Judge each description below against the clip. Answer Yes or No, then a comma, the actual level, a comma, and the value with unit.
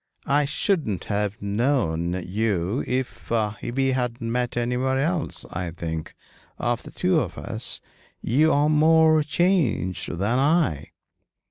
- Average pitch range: No, wide, 6.6 semitones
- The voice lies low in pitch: Yes, low, 125 Hz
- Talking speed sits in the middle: No, slow, 125 wpm